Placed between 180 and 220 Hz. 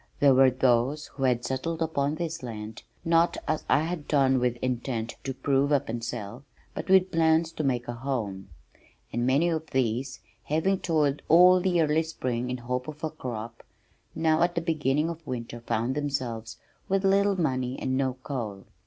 No: low, 135 Hz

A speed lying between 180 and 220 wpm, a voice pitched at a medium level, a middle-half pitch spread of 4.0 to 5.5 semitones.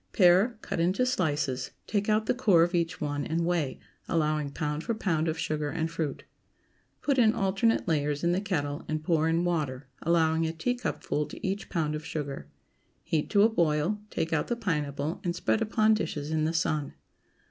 Yes: average, 190 wpm; medium, 165 Hz; average, 4.3 semitones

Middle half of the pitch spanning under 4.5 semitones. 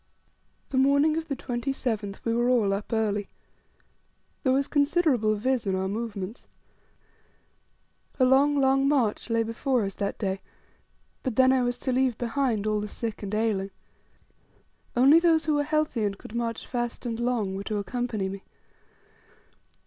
Yes: average, 4.1 semitones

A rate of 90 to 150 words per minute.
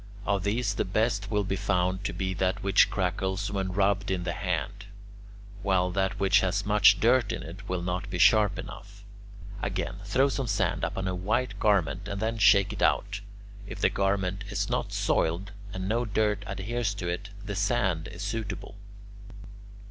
No: average, 180 wpm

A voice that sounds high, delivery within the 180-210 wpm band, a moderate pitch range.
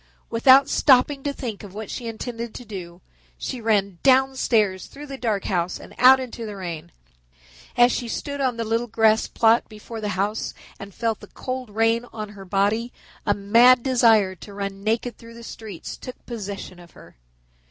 Yes: high, 225 Hz; average, 185 wpm; average, 3.4 semitones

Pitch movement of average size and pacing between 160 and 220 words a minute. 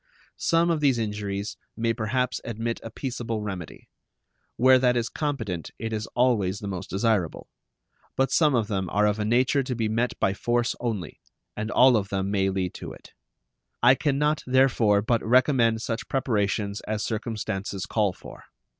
Yes: average, 3.7 semitones; average, 170 wpm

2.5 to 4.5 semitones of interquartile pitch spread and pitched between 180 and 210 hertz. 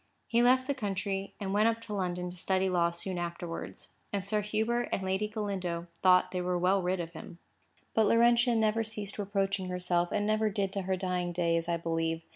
Yes: average, 3.2 semitones; high, 190 Hz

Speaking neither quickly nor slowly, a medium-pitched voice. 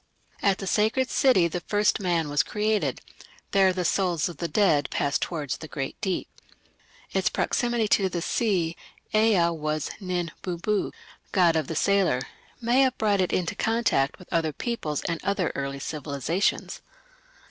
Yes: average, 160 wpm; medium, 180 Hz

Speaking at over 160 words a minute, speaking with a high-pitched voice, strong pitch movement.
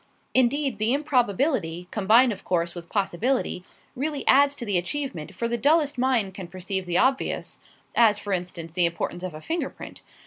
Yes: average, 175 wpm; high, 215 Hz; wide, 6.7 semitones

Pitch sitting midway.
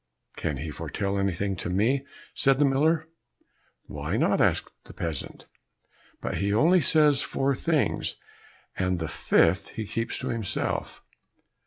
No: low, 110 Hz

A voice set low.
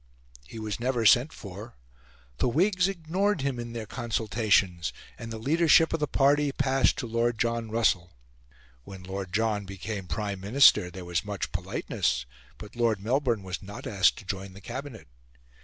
Yes: low, 115 Hz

